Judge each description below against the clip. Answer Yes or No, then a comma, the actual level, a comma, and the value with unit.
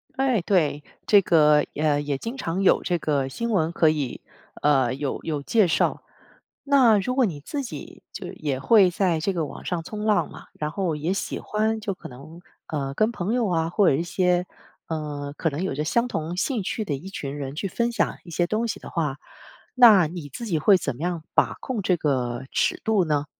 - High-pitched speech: No, medium, 175 Hz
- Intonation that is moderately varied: No, wide, 6.0 semitones